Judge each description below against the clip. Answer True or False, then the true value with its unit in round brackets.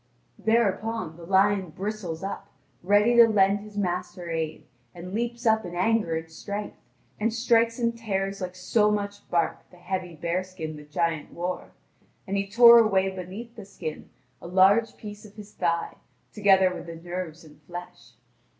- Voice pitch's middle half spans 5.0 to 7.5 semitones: False (3.5 semitones)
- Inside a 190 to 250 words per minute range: False (170 wpm)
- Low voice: False (190 Hz)